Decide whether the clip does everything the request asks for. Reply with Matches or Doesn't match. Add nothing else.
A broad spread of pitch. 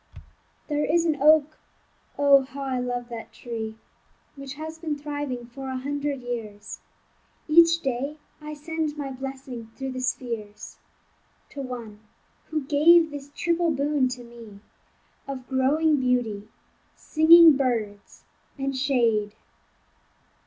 Doesn't match